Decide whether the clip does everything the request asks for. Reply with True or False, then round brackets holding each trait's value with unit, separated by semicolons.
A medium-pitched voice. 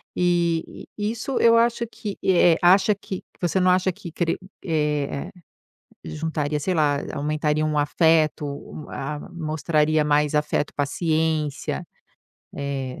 True (155 Hz)